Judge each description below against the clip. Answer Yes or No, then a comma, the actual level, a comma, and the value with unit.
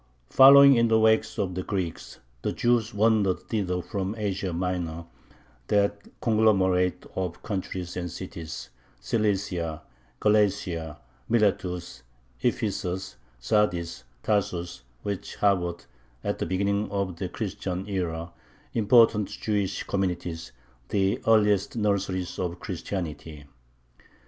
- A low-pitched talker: Yes, very low, 95 Hz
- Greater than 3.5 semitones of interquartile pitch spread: No, average, 2.9 semitones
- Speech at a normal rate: No, slow, 105 wpm